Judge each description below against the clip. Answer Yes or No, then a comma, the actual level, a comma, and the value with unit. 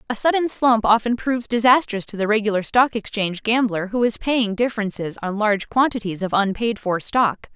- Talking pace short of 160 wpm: No, average, 185 wpm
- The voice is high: Yes, high, 220 Hz